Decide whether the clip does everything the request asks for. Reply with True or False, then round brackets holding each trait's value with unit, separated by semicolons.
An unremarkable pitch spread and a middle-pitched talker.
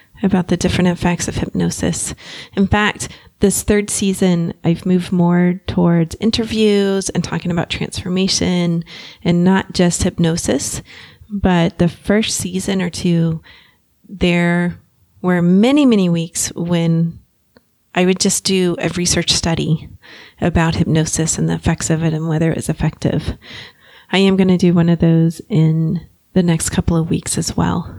False (2.3 semitones; 175 Hz)